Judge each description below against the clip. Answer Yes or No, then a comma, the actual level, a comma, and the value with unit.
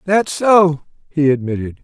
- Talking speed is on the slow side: Yes, slow, 130 wpm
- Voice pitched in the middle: Yes, medium, 155 Hz